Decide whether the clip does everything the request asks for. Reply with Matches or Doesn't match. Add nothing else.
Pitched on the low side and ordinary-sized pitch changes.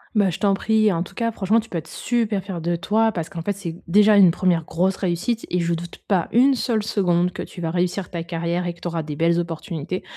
Doesn't match